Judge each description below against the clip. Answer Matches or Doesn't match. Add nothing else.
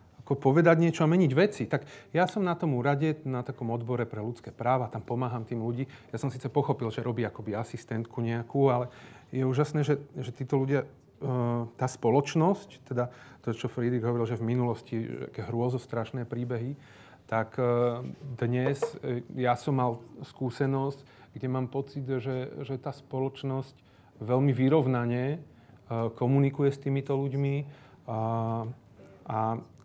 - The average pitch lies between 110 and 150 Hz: Matches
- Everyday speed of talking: Matches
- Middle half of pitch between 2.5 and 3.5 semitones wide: Matches